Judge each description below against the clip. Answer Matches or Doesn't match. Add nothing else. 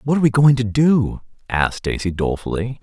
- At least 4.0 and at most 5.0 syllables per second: Doesn't match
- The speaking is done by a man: Matches